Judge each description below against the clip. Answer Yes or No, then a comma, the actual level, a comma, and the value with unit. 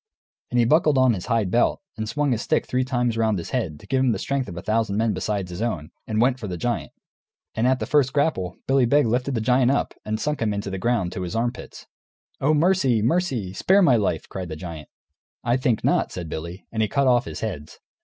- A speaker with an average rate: No, fast, 245 wpm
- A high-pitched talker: No, low, 115 Hz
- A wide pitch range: No, average, 4.7 semitones